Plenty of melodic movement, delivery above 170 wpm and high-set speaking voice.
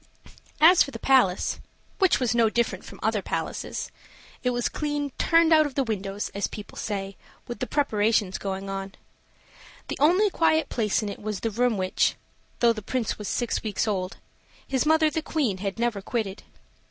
Yes: wide, 6.2 semitones; average, 180 wpm; high, 230 Hz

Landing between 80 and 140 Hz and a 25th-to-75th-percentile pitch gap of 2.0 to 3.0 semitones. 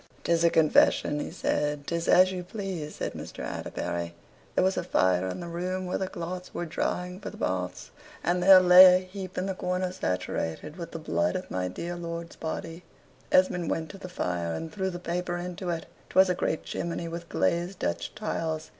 No: medium, 175 Hz; narrow, 2.5 semitones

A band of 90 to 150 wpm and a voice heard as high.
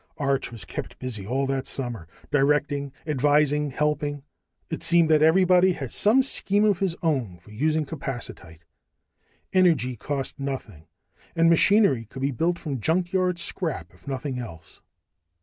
No: average, 145 wpm; medium, 145 Hz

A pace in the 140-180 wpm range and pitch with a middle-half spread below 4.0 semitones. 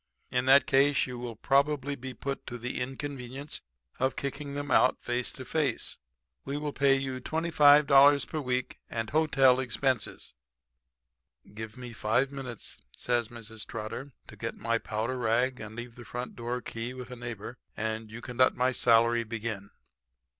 Yes: average, 165 wpm; average, 2.9 semitones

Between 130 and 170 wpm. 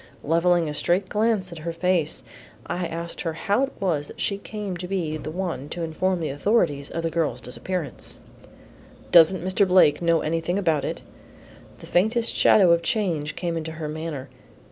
No: average, 185 wpm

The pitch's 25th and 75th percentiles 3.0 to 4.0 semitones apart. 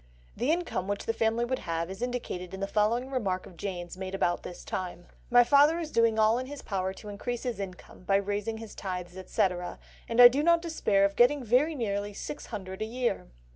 No: average, 4.5 semitones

